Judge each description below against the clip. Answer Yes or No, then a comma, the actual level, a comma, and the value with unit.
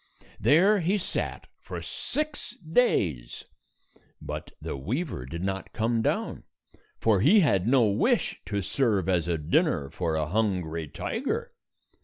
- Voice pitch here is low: Yes, low, 105 Hz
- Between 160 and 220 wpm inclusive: No, average, 140 wpm